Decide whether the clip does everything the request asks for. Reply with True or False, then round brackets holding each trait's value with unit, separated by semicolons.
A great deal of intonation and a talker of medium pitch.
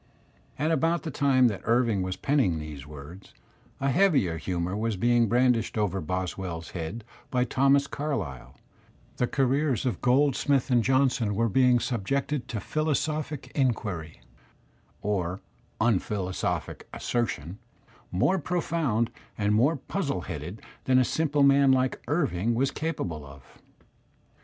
False (6.6 semitones; 120 Hz)